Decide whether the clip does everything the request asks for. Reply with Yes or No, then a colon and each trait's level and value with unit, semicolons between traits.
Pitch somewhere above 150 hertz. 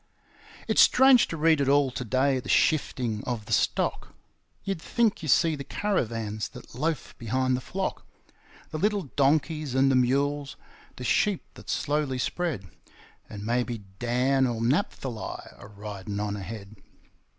No: low, 130 Hz